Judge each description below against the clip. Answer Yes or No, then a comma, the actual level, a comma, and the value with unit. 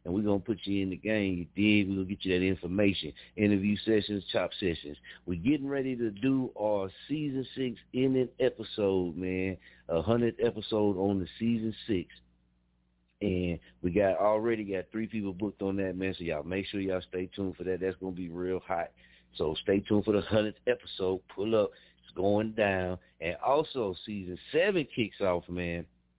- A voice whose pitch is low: Yes, very low, 95 Hz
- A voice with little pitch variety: No, average, 3.1 semitones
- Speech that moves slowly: No, average, 190 wpm